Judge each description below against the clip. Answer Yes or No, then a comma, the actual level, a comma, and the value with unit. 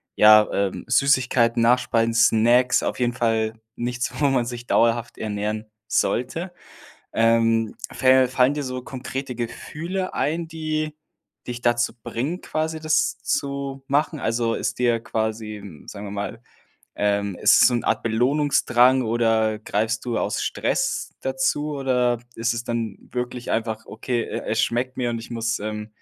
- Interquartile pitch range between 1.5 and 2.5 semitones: No, average, 2.9 semitones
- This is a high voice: No, low, 120 Hz